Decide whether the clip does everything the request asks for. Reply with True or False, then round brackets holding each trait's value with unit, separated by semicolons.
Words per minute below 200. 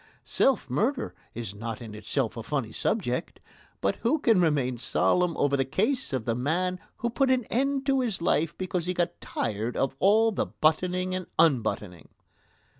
True (175 wpm)